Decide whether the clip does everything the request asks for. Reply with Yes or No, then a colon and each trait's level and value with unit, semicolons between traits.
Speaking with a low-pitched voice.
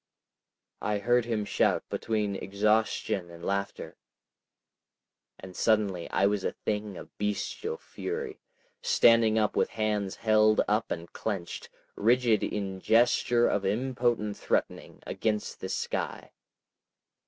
Yes: low, 105 Hz